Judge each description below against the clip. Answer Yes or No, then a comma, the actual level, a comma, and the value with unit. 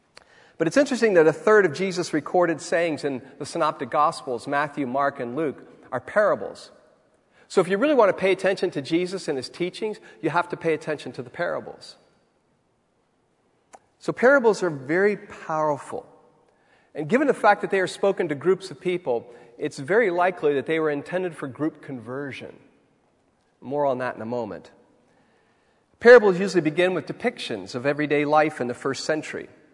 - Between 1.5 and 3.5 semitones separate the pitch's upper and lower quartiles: No, average, 4.5 semitones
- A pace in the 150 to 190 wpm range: Yes, average, 175 wpm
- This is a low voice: No, medium, 160 Hz